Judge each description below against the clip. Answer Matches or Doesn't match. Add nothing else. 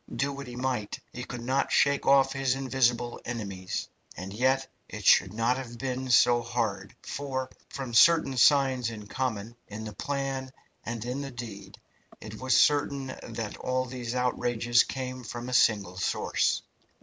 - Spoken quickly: Doesn't match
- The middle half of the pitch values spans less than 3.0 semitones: Matches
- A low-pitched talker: Matches